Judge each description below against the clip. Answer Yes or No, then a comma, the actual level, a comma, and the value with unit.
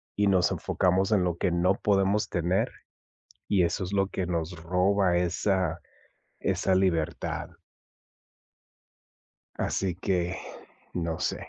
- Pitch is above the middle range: No, very low, 90 Hz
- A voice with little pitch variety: Yes, narrow, 1.9 semitones